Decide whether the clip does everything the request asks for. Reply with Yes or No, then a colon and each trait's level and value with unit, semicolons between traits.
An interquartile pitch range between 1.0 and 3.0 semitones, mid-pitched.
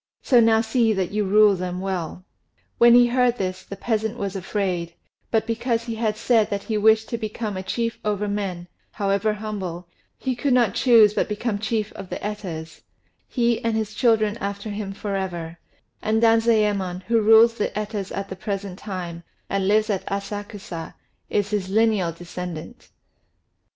No: average, 2.7 semitones; high, 210 Hz